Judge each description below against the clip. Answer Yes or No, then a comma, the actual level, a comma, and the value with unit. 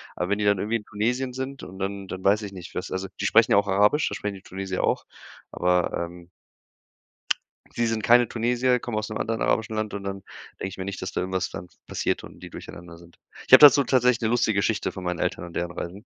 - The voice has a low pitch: Yes, low, 100 Hz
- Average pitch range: Yes, average, 3.5 semitones